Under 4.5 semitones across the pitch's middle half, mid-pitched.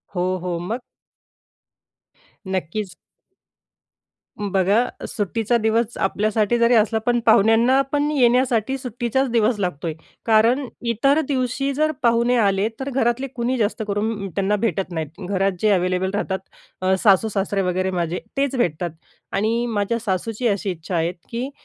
No: average, 3.9 semitones; high, 220 Hz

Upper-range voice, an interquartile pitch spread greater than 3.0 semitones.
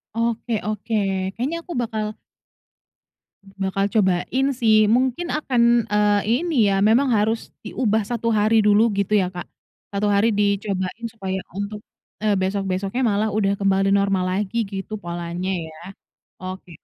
No: high, 205 Hz; average, 2.7 semitones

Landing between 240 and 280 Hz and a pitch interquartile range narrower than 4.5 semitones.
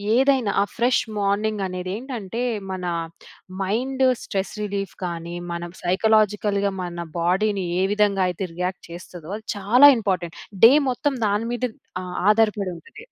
No: high, 200 Hz; average, 3.3 semitones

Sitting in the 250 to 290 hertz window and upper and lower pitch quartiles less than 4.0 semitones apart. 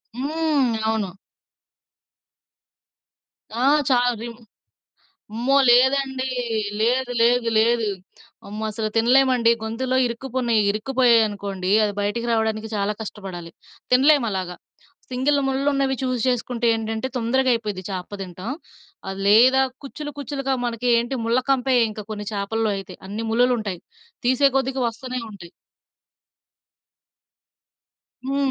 No: high, 235 Hz; average, 3.3 semitones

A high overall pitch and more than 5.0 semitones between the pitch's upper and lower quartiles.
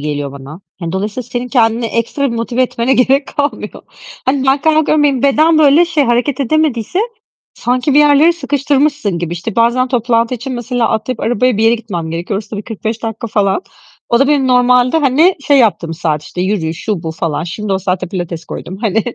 Yes: high, 235 Hz; wide, 5.6 semitones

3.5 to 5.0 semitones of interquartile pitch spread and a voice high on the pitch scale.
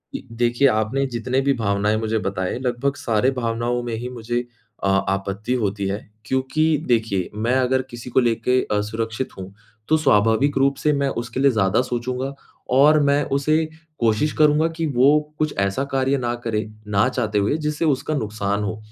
No: average, 4.1 semitones; low, 120 Hz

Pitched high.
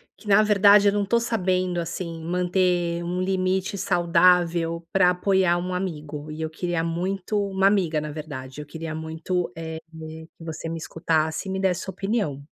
No: medium, 175 Hz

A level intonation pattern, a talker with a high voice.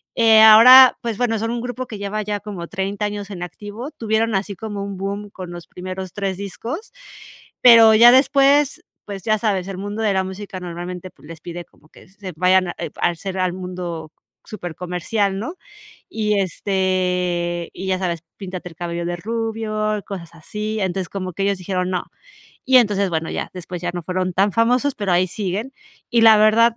No: average, 3.3 semitones; high, 195 Hz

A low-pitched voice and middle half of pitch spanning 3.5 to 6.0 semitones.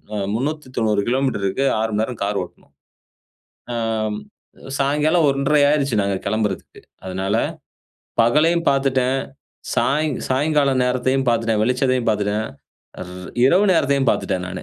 Yes: low, 130 Hz; average, 4.6 semitones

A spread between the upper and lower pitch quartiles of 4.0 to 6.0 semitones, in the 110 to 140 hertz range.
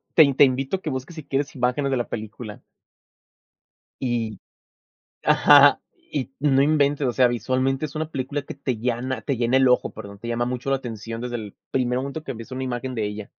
No: narrow, 2.6 semitones; low, 130 Hz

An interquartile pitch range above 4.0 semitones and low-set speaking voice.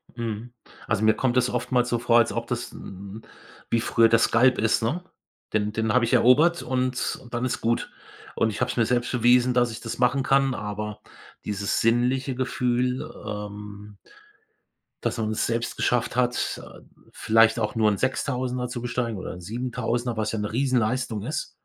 No: narrow, 2.4 semitones; low, 120 Hz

